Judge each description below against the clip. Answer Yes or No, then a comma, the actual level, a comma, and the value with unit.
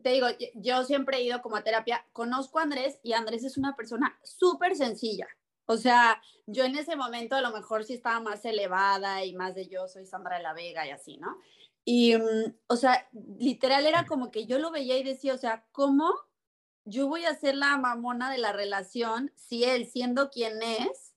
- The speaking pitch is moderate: No, high, 245 Hz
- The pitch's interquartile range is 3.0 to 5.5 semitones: Yes, average, 3.5 semitones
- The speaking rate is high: Yes, fast, 210 wpm